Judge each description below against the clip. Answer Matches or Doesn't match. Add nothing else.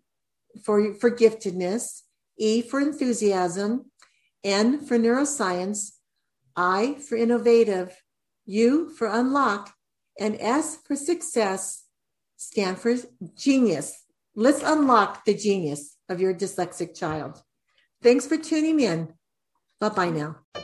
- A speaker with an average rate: Doesn't match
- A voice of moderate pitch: Doesn't match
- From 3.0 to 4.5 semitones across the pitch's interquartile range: Doesn't match